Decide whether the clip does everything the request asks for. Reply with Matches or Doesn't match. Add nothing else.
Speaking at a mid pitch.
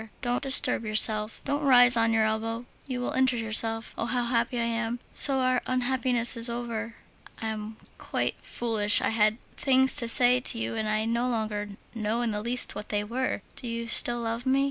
Doesn't match